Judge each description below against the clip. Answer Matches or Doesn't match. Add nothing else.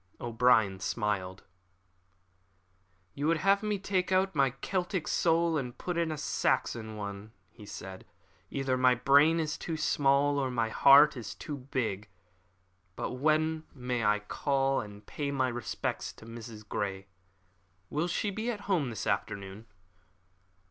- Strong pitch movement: Matches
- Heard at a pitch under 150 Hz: Matches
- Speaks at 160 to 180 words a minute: Doesn't match